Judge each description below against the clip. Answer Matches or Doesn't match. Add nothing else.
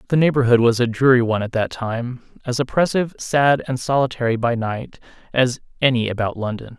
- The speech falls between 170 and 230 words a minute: Matches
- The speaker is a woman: Doesn't match